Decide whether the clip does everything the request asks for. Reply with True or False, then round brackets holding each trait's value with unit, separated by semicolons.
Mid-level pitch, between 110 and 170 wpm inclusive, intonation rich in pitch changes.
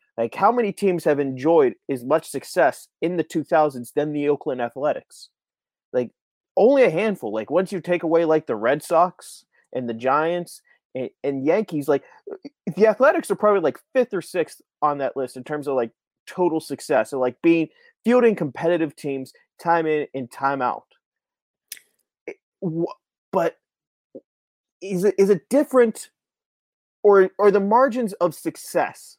True (165 Hz; 160 wpm; 6.1 semitones)